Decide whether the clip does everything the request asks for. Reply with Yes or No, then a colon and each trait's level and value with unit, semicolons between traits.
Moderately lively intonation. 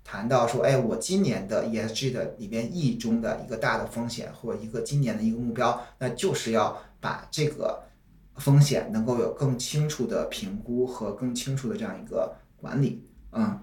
Yes: average, 4.5 semitones